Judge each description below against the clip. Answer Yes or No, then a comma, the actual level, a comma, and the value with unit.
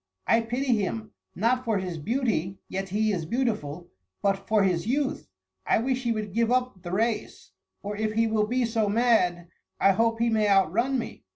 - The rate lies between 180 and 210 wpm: Yes, average, 190 wpm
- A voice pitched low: No, high, 220 Hz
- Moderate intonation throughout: Yes, average, 3.3 semitones